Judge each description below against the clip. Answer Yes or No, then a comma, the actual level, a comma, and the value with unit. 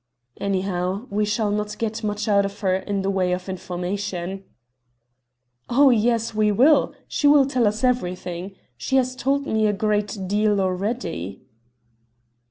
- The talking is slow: No, average, 150 wpm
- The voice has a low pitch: No, high, 205 Hz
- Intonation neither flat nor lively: Yes, average, 3.1 semitones